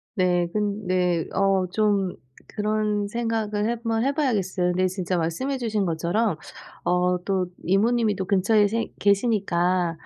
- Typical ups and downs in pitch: Yes, average, 3.3 semitones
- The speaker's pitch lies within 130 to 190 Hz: No, high, 200 Hz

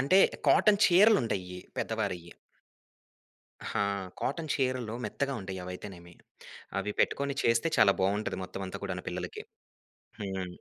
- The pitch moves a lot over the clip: Yes, wide, 6.7 semitones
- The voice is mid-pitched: No, low, 105 Hz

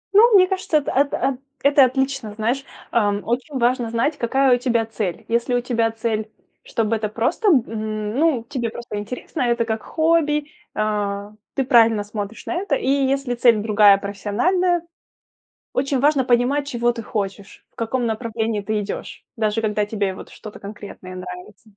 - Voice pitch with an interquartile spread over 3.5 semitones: Yes, average, 4.1 semitones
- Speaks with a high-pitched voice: Yes, high, 235 Hz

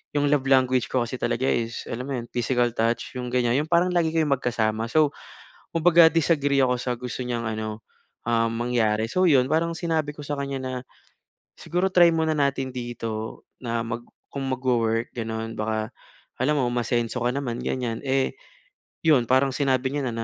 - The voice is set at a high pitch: No, low, 125 Hz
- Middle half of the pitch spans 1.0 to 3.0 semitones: No, average, 3.4 semitones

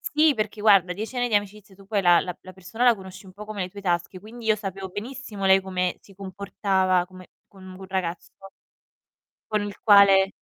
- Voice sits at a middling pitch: No, high, 195 Hz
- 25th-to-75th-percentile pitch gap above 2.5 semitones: No, narrow, 2.2 semitones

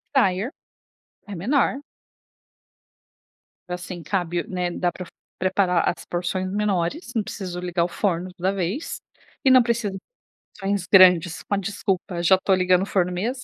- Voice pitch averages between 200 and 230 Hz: No, medium, 185 Hz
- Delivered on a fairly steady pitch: Yes, narrow, 2.3 semitones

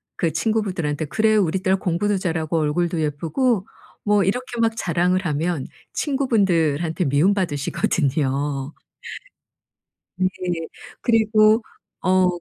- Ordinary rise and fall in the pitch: Yes, average, 5.0 semitones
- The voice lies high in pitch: No, medium, 180 Hz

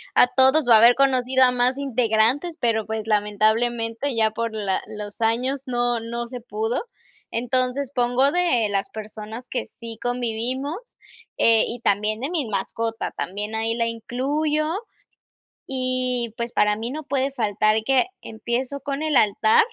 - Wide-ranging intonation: No, average, 3.0 semitones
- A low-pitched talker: No, high, 240 Hz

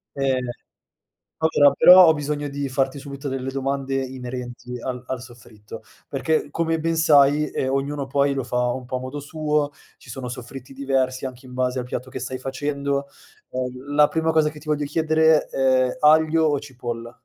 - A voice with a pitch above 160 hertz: No, low, 135 Hz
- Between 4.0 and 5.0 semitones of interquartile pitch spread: No, narrow, 2.5 semitones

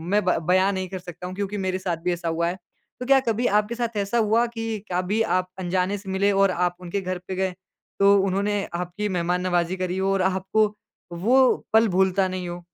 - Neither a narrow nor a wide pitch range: No, narrow, 2.1 semitones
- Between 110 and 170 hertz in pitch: No, high, 190 Hz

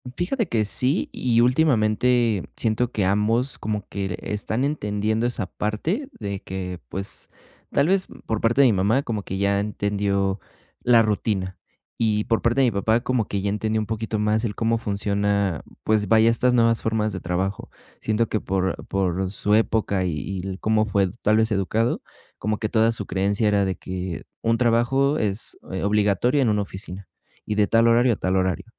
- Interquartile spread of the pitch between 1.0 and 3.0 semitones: Yes, narrow, 2.6 semitones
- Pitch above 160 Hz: No, low, 105 Hz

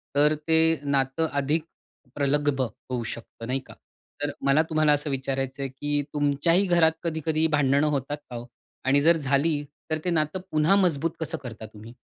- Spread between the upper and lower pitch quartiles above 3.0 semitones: No, average, 2.7 semitones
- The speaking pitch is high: No, medium, 145 Hz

